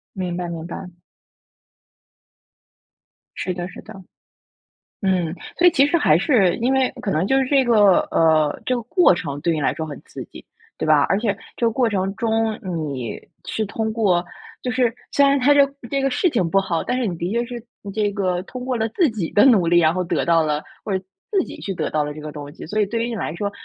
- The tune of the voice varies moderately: No, wide, 6.1 semitones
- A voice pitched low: No, high, 200 Hz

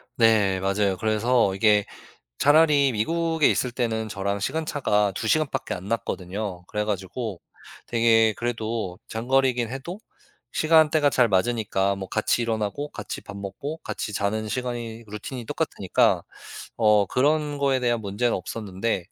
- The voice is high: No, low, 115 Hz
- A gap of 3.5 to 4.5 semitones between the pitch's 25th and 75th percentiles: Yes, average, 4.2 semitones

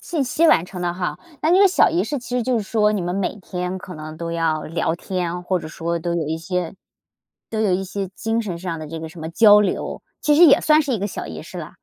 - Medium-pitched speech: Yes, medium, 180 Hz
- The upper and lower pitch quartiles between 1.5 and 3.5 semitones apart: No, average, 4.6 semitones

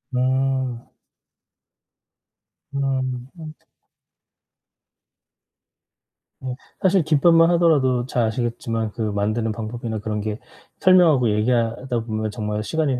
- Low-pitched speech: Yes, low, 125 Hz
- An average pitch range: Yes, average, 3.9 semitones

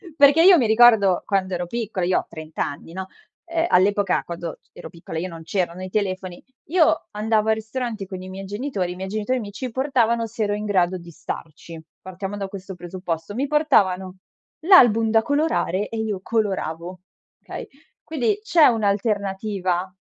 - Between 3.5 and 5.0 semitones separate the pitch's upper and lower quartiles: Yes, average, 3.8 semitones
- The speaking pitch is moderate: No, high, 200 Hz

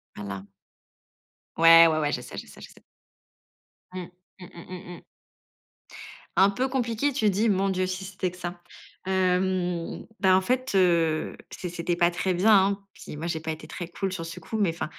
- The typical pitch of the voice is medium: Yes, medium, 180 Hz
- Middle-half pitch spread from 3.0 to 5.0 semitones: No, narrow, 2.5 semitones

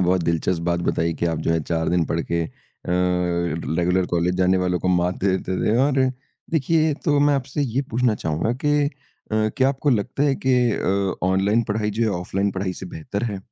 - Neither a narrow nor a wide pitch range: No, wide, 6.4 semitones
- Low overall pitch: Yes, very low, 95 Hz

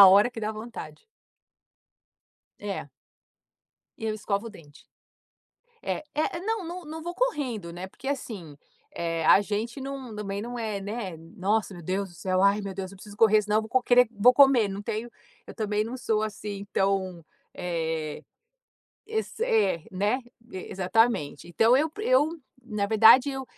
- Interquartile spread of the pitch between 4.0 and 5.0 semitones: Yes, average, 4.3 semitones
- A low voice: No, high, 215 Hz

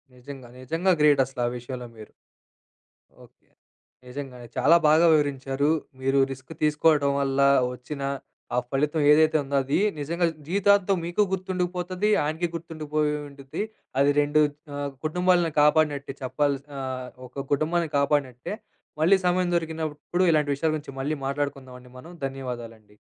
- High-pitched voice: No, medium, 145 Hz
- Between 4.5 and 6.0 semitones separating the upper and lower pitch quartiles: No, average, 3.2 semitones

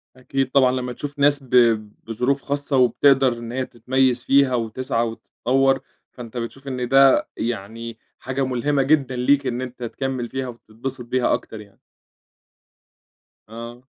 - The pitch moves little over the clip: Yes, narrow, 2.3 semitones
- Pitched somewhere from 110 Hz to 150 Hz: Yes, low, 130 Hz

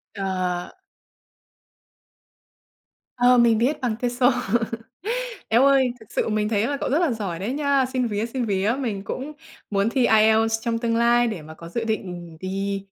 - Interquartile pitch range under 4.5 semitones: Yes, average, 3.8 semitones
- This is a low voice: No, high, 225 Hz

